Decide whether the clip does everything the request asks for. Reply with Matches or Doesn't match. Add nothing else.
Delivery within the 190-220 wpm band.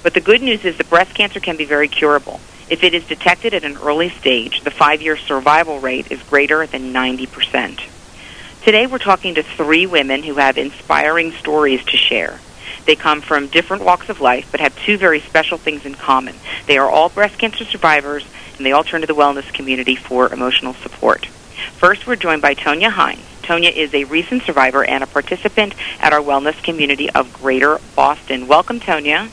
Matches